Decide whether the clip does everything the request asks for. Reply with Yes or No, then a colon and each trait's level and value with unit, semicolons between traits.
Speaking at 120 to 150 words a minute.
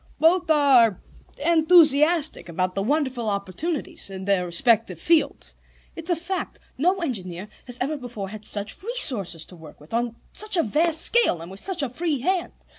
No: average, 170 wpm